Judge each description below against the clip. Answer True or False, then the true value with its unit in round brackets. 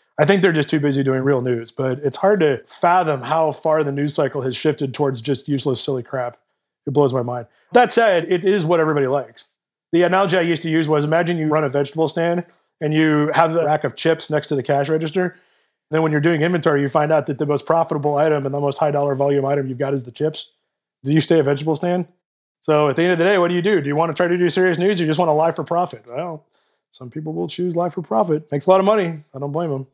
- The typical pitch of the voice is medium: True (155 Hz)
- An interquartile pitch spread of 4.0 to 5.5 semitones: False (3.2 semitones)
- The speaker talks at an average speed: False (275 wpm)